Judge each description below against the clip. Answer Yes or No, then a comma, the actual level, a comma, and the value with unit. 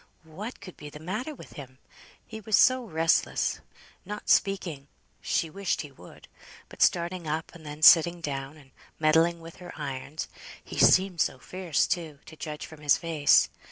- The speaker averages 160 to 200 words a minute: Yes, average, 170 wpm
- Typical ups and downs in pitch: Yes, average, 3.5 semitones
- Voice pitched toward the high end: No, medium, 165 Hz